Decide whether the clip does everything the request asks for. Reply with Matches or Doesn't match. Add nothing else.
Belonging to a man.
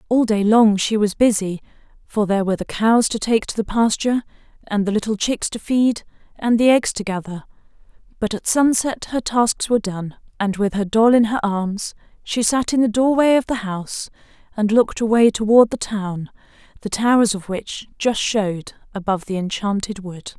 Doesn't match